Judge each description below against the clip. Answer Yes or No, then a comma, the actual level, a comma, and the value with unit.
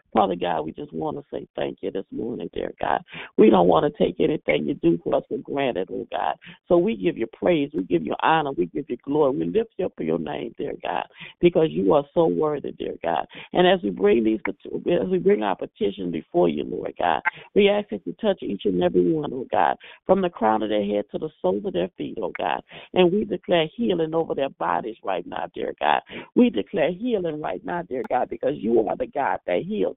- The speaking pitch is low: No, medium, 165 Hz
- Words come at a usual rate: No, fast, 240 wpm